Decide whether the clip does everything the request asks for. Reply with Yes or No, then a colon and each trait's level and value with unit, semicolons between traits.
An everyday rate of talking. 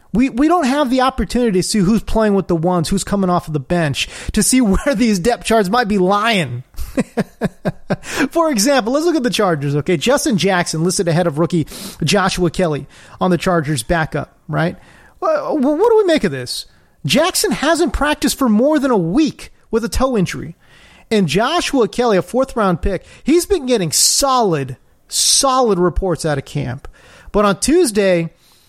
Yes: average, 180 wpm